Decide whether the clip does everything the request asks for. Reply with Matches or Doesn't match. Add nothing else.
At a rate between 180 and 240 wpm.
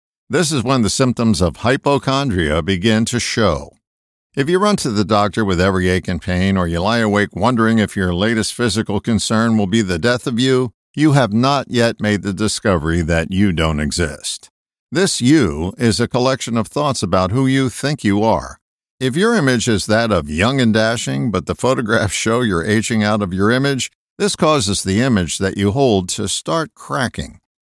Matches